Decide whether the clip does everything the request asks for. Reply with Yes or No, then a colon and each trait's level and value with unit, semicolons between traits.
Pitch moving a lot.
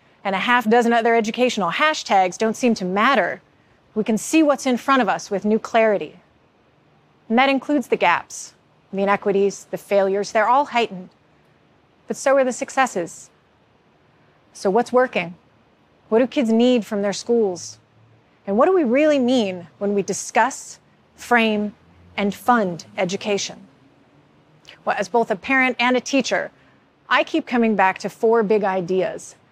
No: average, 4.1 semitones